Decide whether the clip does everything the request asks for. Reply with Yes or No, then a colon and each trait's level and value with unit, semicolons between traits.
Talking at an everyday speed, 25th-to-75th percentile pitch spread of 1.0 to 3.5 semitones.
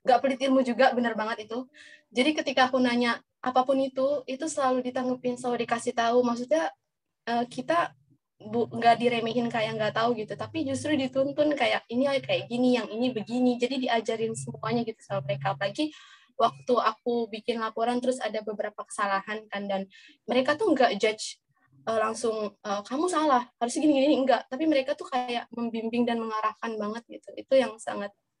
No: fast, 160 wpm; average, 3.2 semitones